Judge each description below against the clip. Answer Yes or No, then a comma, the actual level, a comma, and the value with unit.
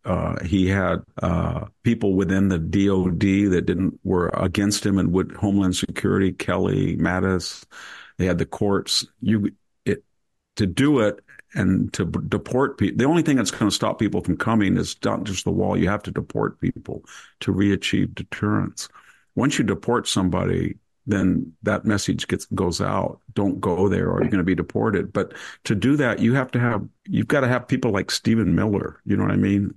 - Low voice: Yes, low, 100 Hz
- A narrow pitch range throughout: No, average, 3.2 semitones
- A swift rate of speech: No, average, 190 wpm